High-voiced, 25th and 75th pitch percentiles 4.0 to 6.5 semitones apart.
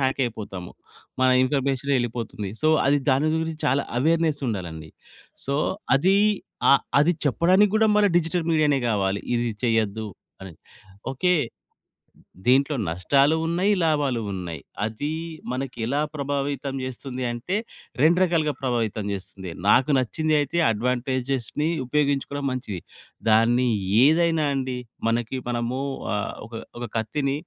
No: low, 130 Hz; average, 4.6 semitones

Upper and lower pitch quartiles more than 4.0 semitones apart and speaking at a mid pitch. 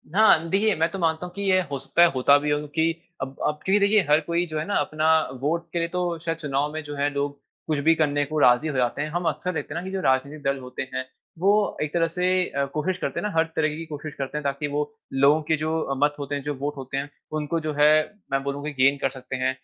No: average, 3.0 semitones; medium, 150 Hz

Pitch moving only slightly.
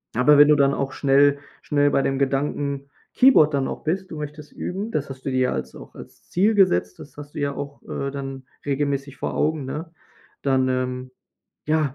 Yes: narrow, 1.8 semitones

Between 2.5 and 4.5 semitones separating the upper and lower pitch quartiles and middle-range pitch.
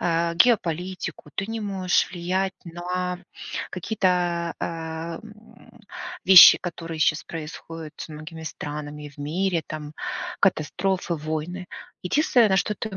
Yes: average, 3.1 semitones; medium, 175 Hz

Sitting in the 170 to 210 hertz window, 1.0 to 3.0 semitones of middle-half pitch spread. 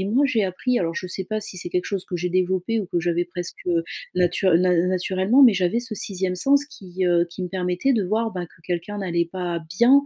No: medium, 185 Hz; average, 3.4 semitones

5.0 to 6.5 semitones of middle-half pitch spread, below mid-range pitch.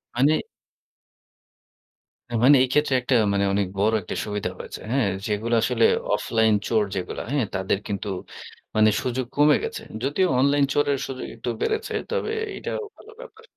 Yes: wide, 5.4 semitones; low, 125 Hz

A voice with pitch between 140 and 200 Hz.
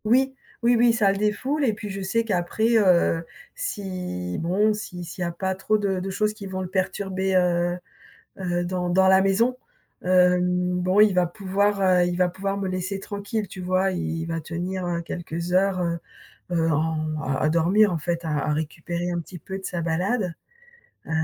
Yes: medium, 185 Hz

